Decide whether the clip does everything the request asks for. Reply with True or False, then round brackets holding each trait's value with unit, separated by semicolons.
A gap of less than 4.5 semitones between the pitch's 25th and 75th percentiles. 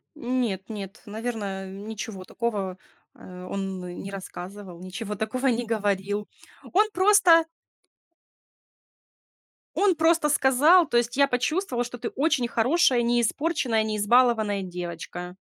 False (5.1 semitones)